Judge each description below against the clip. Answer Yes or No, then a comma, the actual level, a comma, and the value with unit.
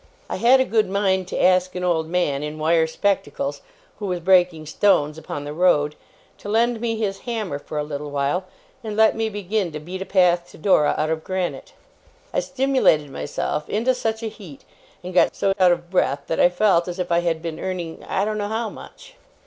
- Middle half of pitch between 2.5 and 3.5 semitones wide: No, average, 4.6 semitones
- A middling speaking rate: No, fast, 215 wpm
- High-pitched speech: No, medium, 180 Hz